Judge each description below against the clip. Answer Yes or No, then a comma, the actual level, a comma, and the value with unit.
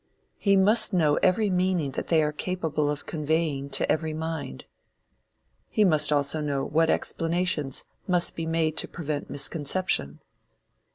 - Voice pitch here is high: No, medium, 160 Hz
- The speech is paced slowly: No, average, 145 wpm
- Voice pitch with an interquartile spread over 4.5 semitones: No, average, 3.5 semitones